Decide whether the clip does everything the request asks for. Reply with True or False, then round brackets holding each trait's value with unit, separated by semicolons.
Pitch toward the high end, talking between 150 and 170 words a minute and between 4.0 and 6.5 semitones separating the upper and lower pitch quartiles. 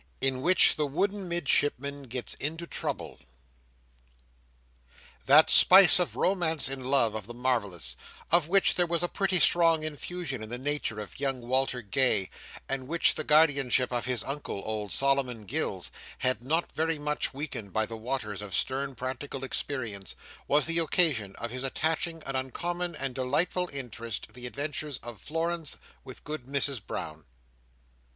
False (135 Hz; 160 wpm; 4.6 semitones)